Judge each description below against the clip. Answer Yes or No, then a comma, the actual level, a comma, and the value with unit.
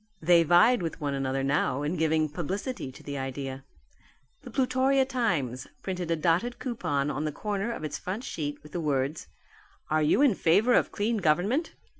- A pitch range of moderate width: No, wide, 7.6 semitones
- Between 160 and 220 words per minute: Yes, average, 180 wpm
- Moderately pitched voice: Yes, medium, 165 Hz